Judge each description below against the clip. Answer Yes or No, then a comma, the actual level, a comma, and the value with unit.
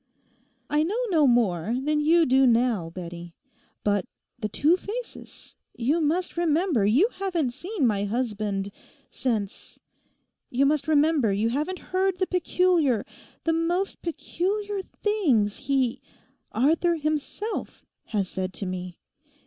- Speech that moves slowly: Yes, slow, 115 wpm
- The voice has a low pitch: No, very high, 280 Hz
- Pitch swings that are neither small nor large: No, wide, 8.3 semitones